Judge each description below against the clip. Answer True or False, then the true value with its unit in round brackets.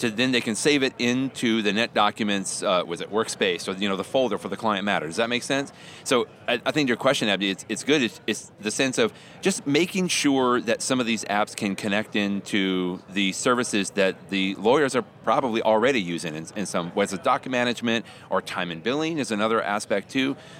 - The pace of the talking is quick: True (225 wpm)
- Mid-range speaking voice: False (110 Hz)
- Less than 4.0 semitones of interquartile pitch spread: False (4.4 semitones)